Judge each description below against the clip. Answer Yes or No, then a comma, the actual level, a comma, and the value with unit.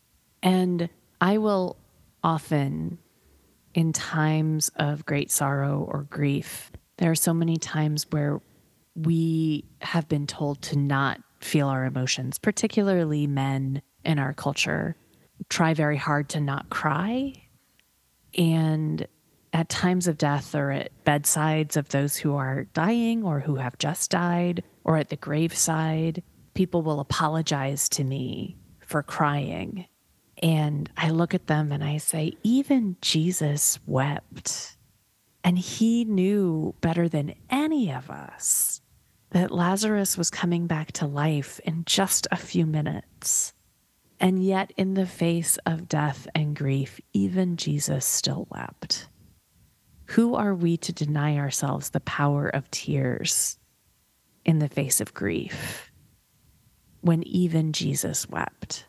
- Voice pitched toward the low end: No, medium, 155 Hz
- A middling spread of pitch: Yes, average, 3.4 semitones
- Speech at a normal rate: No, slow, 130 wpm